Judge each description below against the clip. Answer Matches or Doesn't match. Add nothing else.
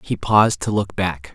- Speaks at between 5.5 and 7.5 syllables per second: Doesn't match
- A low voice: Matches